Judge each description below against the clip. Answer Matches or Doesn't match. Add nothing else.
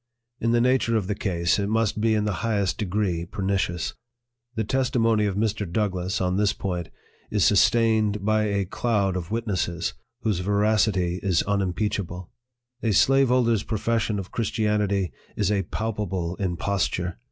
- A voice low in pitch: Matches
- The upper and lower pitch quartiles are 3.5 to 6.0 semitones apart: Doesn't match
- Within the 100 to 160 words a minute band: Matches